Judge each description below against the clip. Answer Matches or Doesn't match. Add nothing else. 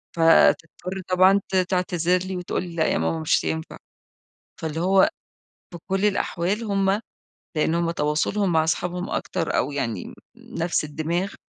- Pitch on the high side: Doesn't match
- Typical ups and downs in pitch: Matches